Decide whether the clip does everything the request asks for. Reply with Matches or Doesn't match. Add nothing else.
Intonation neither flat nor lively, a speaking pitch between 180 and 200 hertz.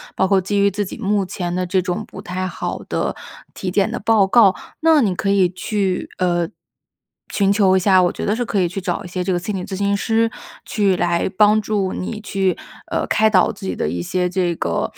Doesn't match